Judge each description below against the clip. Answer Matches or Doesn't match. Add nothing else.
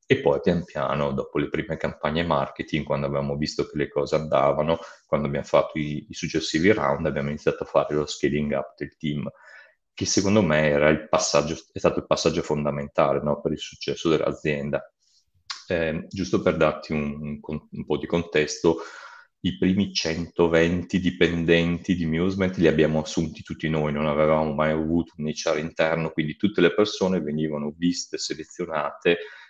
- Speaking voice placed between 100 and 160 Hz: Doesn't match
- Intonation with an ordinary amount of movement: Doesn't match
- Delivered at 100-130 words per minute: Doesn't match